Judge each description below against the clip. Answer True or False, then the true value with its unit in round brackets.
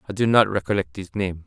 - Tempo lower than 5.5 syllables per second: False (6.1 syllables/s)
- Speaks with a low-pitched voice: True (100 Hz)